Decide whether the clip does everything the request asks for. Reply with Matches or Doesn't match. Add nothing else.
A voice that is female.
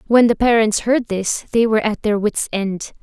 Matches